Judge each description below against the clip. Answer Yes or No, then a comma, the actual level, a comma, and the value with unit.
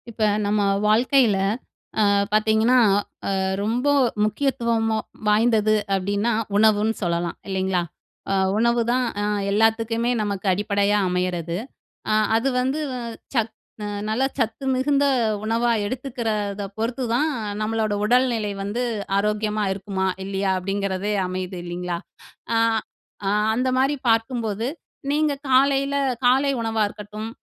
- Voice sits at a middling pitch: No, high, 220 Hz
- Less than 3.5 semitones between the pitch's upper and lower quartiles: Yes, average, 3.1 semitones